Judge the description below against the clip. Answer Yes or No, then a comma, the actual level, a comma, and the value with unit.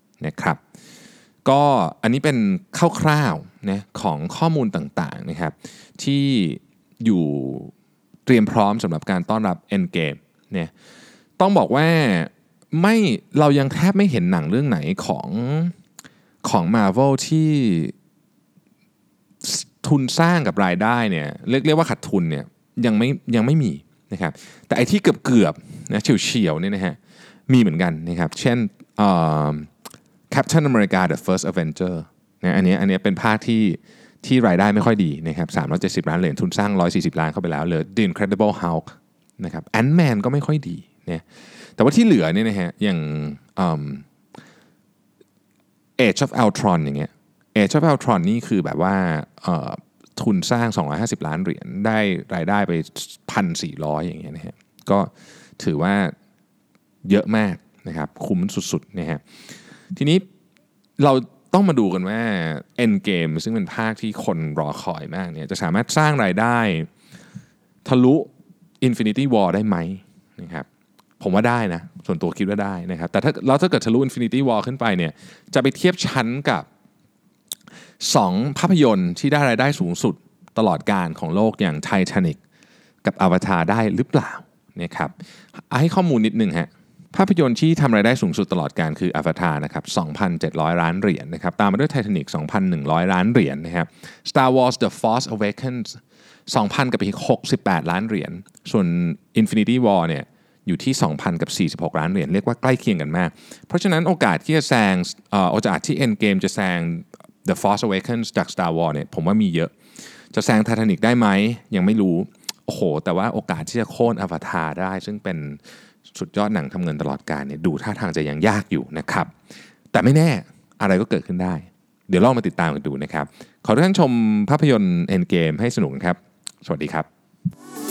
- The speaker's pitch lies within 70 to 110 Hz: No, low, 120 Hz